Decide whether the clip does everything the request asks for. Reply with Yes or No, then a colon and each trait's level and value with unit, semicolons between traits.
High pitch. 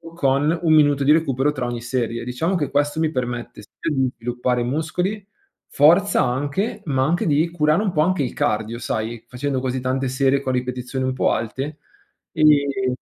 No: low, 135 Hz